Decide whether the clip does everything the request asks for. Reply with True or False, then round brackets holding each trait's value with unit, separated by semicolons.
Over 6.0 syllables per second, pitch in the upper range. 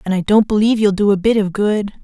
True (6.5 syllables/s; 205 Hz)